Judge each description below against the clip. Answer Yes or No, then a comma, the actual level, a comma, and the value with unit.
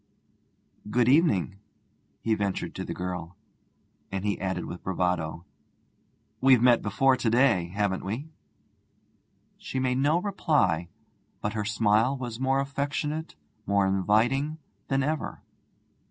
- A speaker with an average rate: No, slow, 125 wpm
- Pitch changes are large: Yes, wide, 5.8 semitones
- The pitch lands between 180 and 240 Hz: No, low, 115 Hz